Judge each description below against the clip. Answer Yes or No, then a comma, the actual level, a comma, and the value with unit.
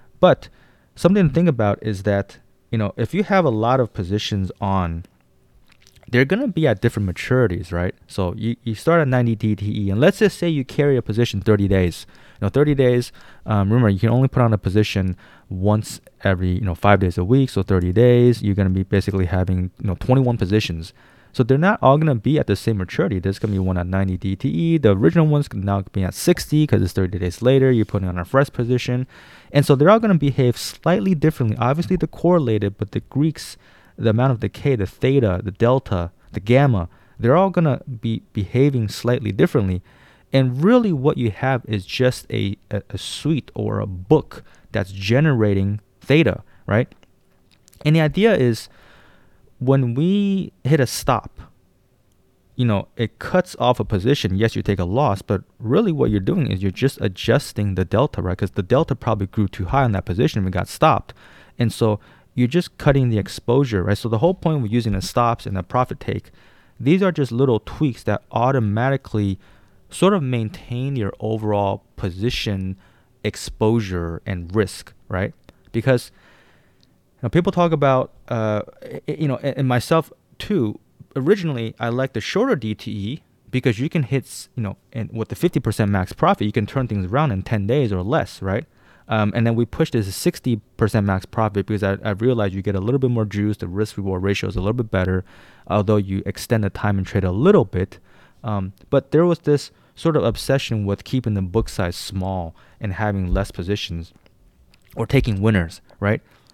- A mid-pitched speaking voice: No, low, 110 Hz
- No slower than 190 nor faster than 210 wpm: Yes, average, 195 wpm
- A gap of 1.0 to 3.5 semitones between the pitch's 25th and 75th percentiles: No, wide, 5.4 semitones